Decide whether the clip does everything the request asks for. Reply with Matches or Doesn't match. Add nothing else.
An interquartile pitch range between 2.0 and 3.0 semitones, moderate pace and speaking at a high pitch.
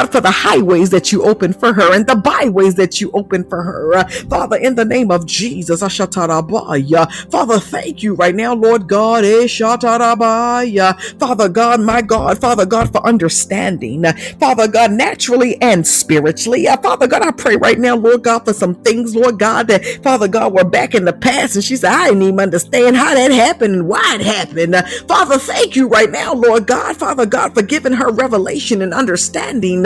Doesn't match